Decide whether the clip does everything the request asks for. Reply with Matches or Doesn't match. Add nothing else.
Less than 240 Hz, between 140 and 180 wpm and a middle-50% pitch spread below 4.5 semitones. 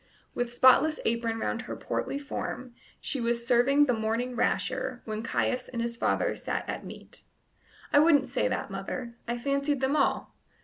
Doesn't match